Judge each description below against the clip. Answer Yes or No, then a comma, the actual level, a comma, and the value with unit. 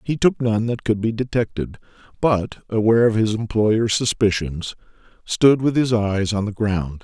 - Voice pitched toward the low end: Yes, low, 110 Hz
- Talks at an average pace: Yes, average, 170 wpm